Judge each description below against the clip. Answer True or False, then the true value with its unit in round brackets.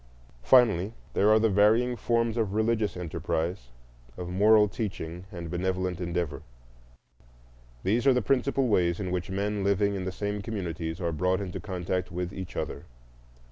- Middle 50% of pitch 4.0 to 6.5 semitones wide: False (3.3 semitones)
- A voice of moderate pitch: False (95 Hz)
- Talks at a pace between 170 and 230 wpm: False (155 wpm)